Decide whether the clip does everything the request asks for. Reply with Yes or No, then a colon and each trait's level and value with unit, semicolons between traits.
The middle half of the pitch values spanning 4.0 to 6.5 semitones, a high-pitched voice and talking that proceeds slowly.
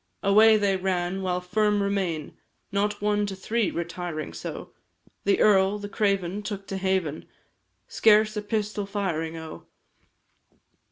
No: narrow, 2.5 semitones; high, 195 Hz; slow, 130 wpm